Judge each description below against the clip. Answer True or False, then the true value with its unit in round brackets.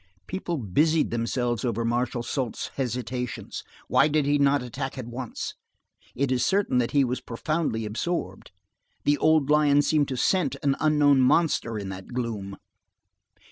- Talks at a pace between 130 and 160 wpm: True (150 wpm)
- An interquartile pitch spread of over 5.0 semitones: False (3.7 semitones)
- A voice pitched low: True (130 Hz)